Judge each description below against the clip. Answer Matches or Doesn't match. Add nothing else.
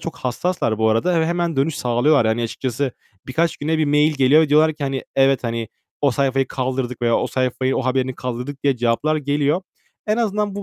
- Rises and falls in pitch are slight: Doesn't match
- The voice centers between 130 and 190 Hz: Matches